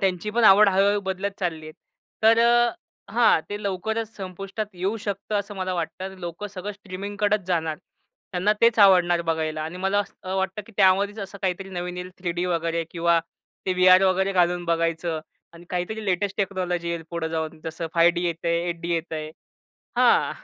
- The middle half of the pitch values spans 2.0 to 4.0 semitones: Yes, average, 2.9 semitones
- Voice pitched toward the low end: No, medium, 185 Hz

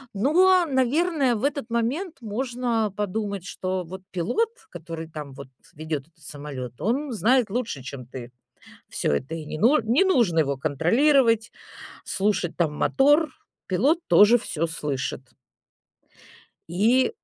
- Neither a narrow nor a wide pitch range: No, wide, 8.5 semitones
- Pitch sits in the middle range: No, high, 205 Hz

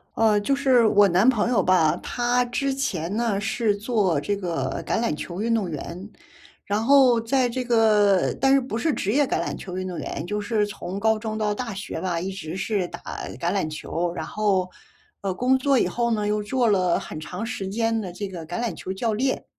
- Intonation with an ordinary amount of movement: Yes, average, 4.1 semitones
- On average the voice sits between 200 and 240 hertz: Yes, high, 210 Hz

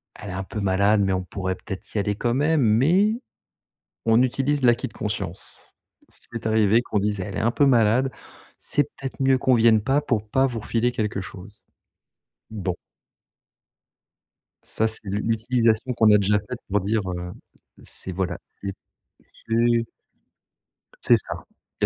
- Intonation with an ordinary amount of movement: Yes, average, 3.4 semitones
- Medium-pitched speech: No, low, 110 Hz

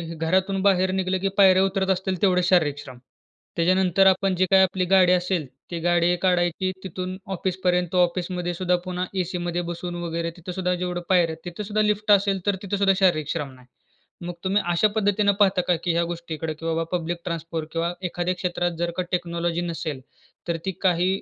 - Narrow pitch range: Yes, narrow, 1.8 semitones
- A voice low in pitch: No, medium, 180 Hz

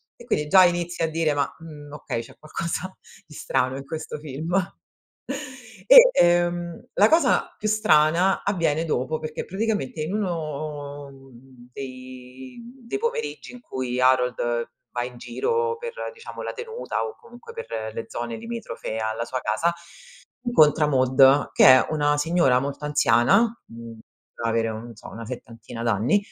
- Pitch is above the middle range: No, medium, 150 Hz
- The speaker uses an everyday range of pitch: No, wide, 6.8 semitones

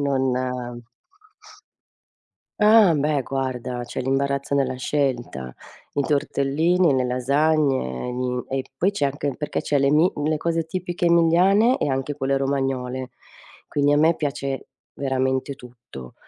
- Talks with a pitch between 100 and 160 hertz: Yes, medium, 140 Hz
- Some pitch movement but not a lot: Yes, average, 3.0 semitones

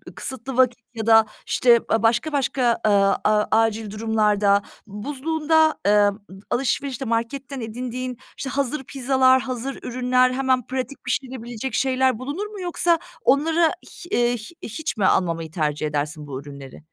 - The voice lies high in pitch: Yes, high, 245 Hz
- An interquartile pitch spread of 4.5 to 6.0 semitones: No, average, 4.0 semitones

